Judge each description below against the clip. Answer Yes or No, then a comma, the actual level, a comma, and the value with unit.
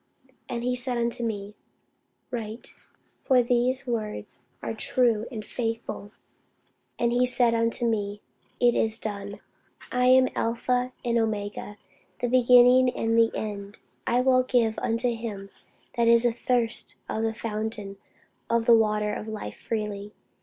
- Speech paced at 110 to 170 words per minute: Yes, average, 140 wpm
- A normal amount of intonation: No, narrow, 2.3 semitones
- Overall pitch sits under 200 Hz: No, high, 230 Hz